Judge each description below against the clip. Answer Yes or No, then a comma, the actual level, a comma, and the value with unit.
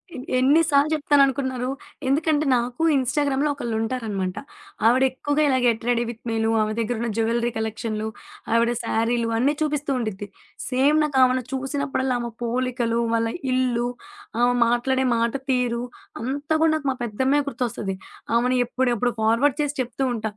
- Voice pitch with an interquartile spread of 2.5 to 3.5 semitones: Yes, average, 2.9 semitones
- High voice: Yes, very high, 250 Hz